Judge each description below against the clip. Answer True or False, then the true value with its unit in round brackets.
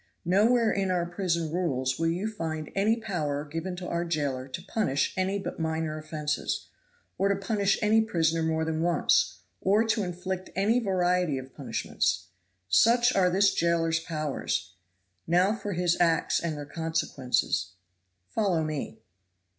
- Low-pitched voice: False (170 Hz)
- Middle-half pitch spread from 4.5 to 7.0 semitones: False (3.8 semitones)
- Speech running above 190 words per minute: False (150 wpm)